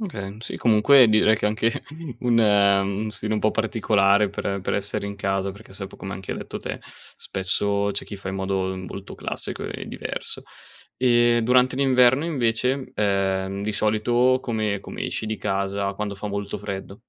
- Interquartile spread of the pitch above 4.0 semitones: No, average, 2.7 semitones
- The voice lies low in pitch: Yes, low, 105 Hz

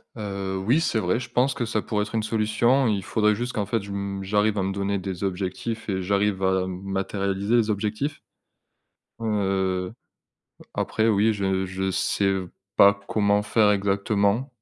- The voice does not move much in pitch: Yes, narrow, 2.2 semitones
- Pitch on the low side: Yes, low, 100 Hz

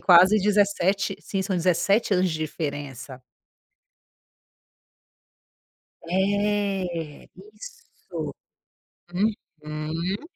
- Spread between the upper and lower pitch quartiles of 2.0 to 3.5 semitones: No, average, 4.1 semitones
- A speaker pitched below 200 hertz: Yes, medium, 185 Hz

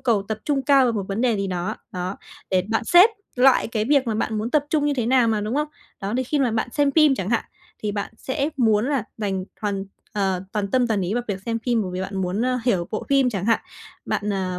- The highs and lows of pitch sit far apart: No, average, 4.6 semitones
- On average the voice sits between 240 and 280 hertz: No, high, 220 Hz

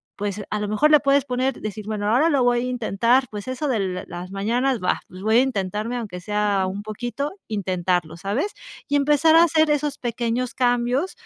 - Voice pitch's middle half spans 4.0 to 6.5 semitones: Yes, average, 4.6 semitones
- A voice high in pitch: Yes, high, 235 Hz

